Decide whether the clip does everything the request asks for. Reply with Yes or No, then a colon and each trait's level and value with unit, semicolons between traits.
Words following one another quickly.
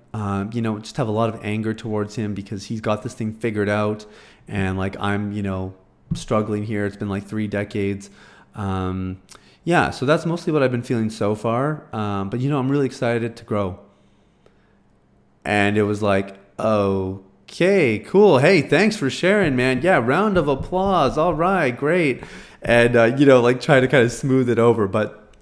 No: average, 190 wpm